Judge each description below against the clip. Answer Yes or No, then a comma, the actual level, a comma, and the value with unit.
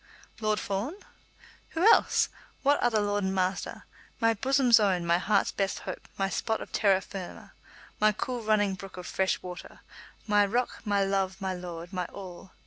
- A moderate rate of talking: Yes, average, 170 wpm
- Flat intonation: Yes, narrow, 2.3 semitones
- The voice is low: No, high, 200 Hz